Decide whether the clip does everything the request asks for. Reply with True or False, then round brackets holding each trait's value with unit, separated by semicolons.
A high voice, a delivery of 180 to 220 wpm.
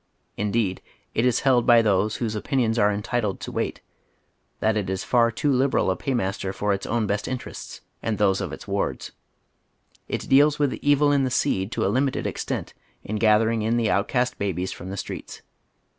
False (110 Hz; 190 wpm)